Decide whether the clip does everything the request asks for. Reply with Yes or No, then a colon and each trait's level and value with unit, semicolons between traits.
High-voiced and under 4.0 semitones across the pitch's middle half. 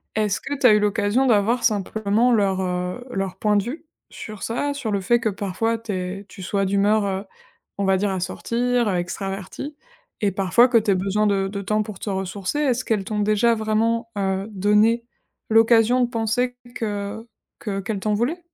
Yes: high, 210 Hz; average, 2.9 semitones